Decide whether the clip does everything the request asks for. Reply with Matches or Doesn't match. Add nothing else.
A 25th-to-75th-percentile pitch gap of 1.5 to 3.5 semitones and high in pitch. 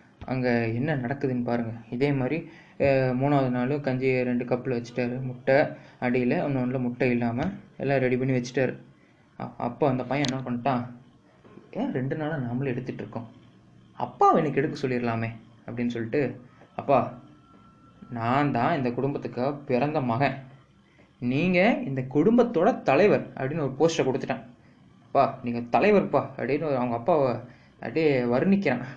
Doesn't match